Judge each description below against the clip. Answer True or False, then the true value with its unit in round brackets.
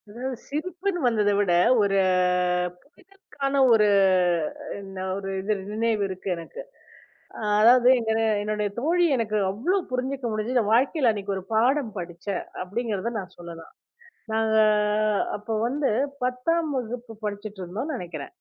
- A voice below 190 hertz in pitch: False (220 Hz)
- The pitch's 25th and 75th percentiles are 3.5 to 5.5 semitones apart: True (4.2 semitones)